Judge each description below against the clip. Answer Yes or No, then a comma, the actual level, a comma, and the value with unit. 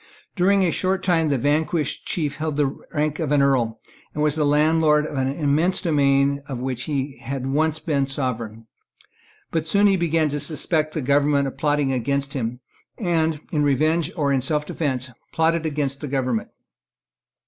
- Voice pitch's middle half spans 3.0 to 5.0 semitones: No, narrow, 2.5 semitones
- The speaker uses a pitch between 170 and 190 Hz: No, medium, 145 Hz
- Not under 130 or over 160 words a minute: No, average, 175 wpm